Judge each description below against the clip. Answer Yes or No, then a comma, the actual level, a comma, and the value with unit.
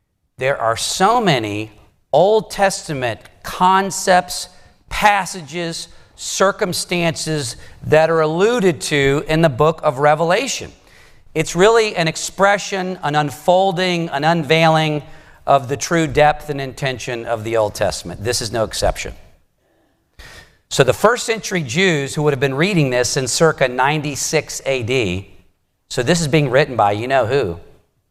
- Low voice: No, medium, 155 Hz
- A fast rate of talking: No, slow, 135 wpm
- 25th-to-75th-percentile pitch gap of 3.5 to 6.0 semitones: Yes, wide, 5.6 semitones